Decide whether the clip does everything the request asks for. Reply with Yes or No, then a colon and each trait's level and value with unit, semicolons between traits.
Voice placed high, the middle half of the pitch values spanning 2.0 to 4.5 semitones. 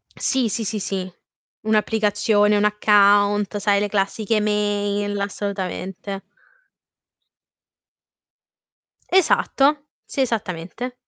No: high, 205 Hz; narrow, 1.4 semitones